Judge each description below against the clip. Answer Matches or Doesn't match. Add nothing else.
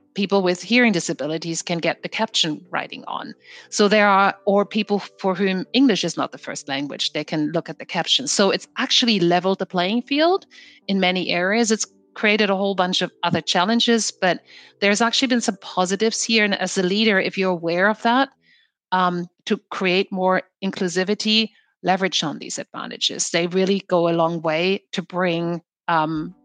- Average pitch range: Matches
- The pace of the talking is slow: Doesn't match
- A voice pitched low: Doesn't match